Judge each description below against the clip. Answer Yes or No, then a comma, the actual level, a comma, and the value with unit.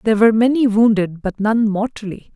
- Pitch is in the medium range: No, high, 215 Hz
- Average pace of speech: Yes, average, 180 wpm